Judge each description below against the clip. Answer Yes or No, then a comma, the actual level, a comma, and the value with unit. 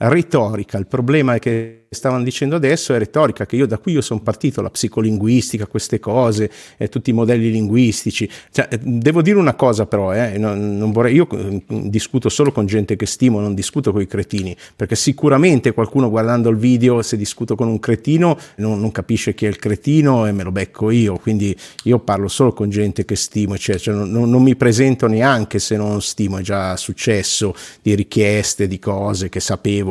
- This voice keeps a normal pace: No, fast, 195 wpm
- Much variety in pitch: No, average, 3.2 semitones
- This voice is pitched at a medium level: No, low, 110 Hz